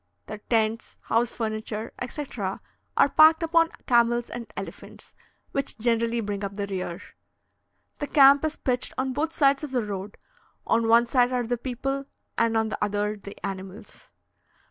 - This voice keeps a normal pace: Yes, average, 160 wpm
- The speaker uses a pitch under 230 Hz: No, high, 235 Hz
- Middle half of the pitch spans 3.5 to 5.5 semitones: Yes, average, 4.2 semitones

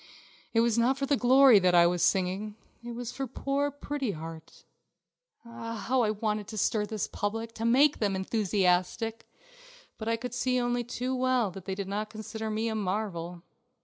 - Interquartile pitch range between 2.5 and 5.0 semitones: Yes, average, 3.7 semitones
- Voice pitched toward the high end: Yes, high, 220 Hz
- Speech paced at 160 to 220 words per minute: Yes, average, 185 wpm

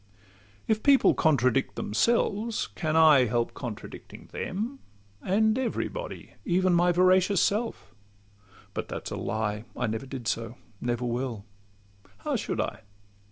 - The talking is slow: Yes, slow, 125 wpm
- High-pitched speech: No, low, 130 Hz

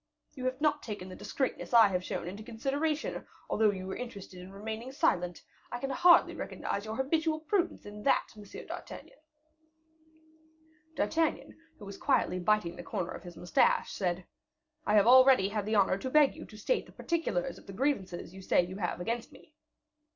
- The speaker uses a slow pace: No, average, 185 wpm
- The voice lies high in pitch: Yes, high, 215 Hz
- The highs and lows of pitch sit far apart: Yes, wide, 6.0 semitones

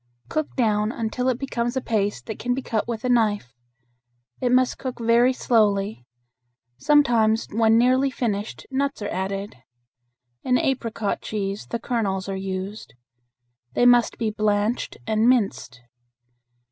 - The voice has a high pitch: Yes, high, 225 Hz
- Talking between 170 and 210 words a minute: No, average, 140 wpm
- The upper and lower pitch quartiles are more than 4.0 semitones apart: No, average, 3.2 semitones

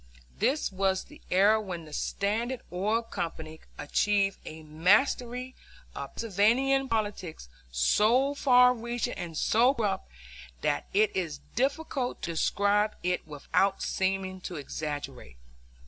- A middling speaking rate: No, slow, 120 wpm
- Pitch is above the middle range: Yes, high, 200 Hz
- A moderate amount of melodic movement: No, wide, 5.9 semitones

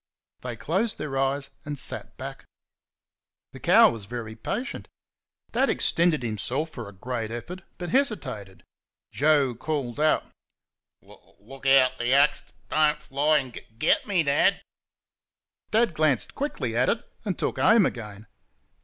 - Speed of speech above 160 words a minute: No, average, 155 wpm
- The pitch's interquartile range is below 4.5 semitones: No, average, 4.8 semitones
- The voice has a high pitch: No, low, 135 Hz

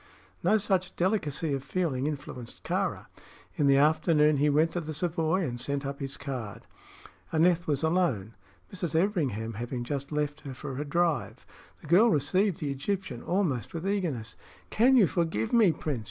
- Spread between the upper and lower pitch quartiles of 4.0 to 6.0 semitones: Yes, average, 4.4 semitones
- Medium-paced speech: Yes, average, 170 wpm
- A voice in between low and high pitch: Yes, medium, 150 Hz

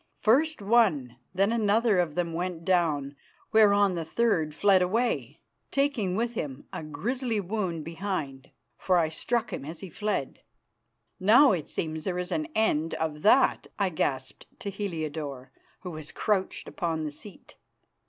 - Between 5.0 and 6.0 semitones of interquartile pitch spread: Yes, average, 5.3 semitones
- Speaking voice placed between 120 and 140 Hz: No, medium, 180 Hz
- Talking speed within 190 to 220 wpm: No, average, 155 wpm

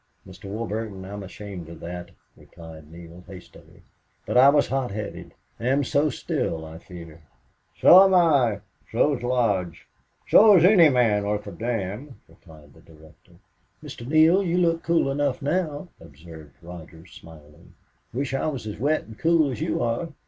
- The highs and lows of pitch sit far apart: Yes, wide, 8.7 semitones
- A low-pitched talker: Yes, low, 110 Hz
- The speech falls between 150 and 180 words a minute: Yes, average, 165 wpm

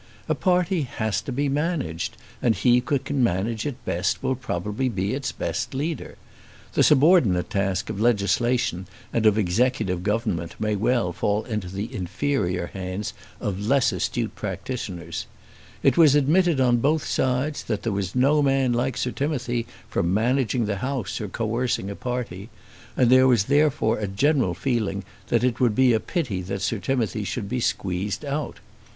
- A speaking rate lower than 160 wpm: No, average, 170 wpm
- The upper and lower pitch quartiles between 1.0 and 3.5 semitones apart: No, average, 5.0 semitones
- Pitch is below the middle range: Yes, low, 120 Hz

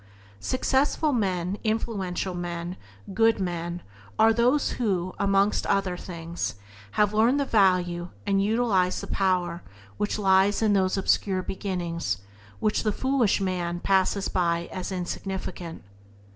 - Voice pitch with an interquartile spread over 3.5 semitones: No, average, 3.1 semitones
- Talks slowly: Yes, slow, 130 wpm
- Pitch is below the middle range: No, high, 190 Hz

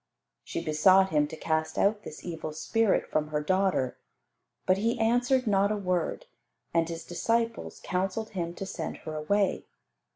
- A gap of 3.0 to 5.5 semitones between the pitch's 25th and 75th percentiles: Yes, average, 4.8 semitones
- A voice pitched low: No, medium, 185 Hz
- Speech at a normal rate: Yes, average, 160 wpm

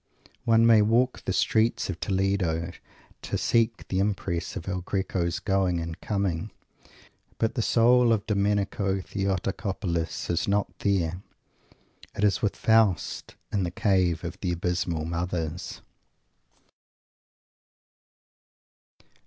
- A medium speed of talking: No, slow, 115 wpm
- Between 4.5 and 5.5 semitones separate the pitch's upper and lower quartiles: No, average, 3.1 semitones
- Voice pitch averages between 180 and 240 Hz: No, very low, 95 Hz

